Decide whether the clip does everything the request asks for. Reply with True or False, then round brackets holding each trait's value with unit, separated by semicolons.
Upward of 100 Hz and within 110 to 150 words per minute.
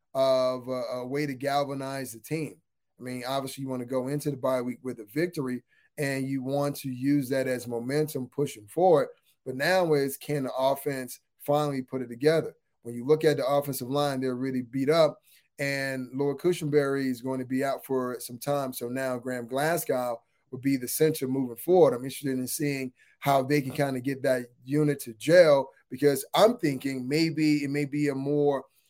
False (135 Hz; 200 wpm)